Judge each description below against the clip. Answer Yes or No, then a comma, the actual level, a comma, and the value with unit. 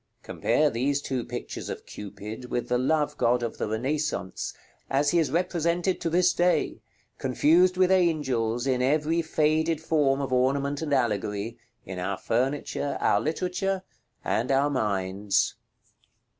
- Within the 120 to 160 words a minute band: Yes, average, 145 wpm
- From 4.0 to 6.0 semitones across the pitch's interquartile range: Yes, average, 5.2 semitones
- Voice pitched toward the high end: No, medium, 140 Hz